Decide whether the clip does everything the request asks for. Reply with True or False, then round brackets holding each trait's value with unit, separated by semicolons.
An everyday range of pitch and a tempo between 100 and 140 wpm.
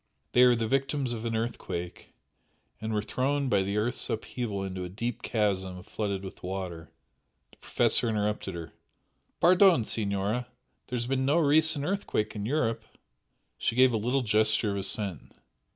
False (4.1 semitones; 165 wpm)